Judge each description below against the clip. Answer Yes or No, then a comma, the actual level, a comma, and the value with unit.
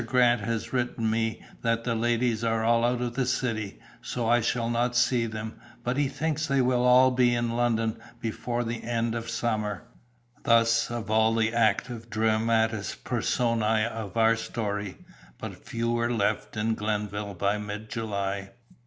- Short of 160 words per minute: No, average, 165 wpm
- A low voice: Yes, low, 115 Hz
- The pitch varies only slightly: Yes, narrow, 1.5 semitones